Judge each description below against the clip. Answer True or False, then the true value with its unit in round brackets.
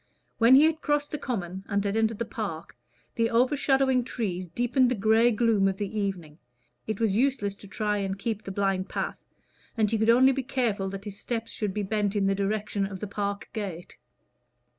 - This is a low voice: False (210 Hz)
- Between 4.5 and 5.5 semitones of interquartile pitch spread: False (3.2 semitones)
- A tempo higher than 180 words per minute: True (205 wpm)